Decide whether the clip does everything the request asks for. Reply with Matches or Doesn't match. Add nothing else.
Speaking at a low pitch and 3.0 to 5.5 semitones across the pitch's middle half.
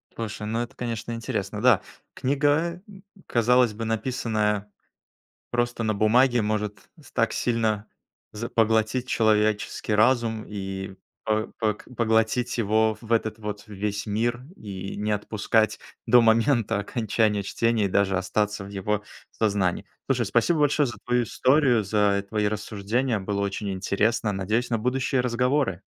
Doesn't match